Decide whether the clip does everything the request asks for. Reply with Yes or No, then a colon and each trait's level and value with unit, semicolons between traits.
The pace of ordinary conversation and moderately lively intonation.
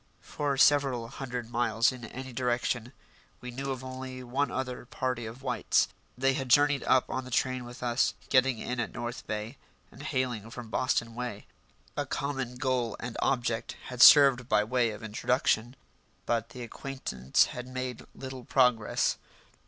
No: average, 160 wpm; narrow, 1.8 semitones